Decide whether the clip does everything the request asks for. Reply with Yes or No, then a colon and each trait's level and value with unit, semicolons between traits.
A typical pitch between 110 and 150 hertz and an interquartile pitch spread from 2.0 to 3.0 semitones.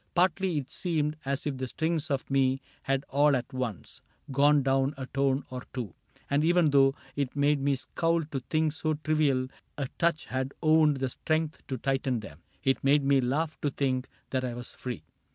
Yes: medium, 140 Hz; narrow, 2.6 semitones